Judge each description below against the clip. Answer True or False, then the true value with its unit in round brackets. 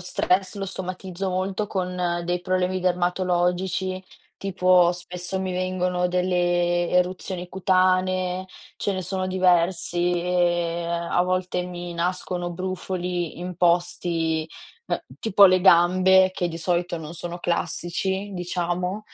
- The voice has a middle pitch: True (180 Hz)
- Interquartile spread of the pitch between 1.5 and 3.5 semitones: False (1.1 semitones)